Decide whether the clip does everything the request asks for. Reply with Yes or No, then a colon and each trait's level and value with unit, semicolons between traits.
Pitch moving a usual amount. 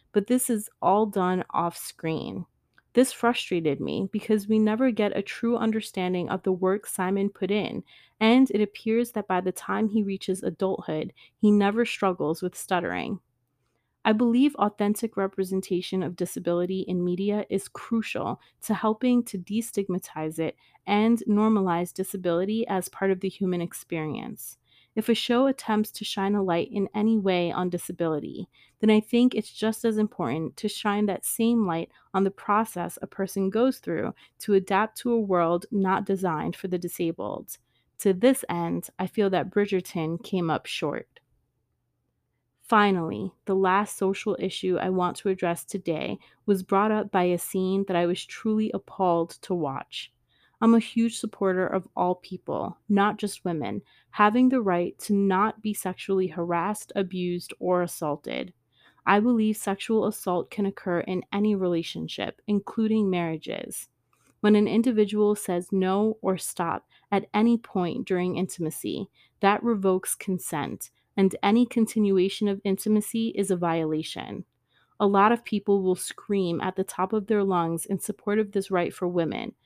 Yes: average, 3.1 semitones